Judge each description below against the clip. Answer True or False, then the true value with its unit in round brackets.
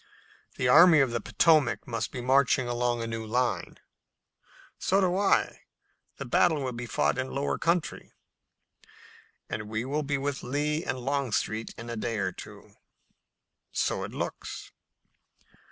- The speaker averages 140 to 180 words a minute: True (155 wpm)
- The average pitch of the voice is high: False (130 Hz)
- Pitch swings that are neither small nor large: True (3.8 semitones)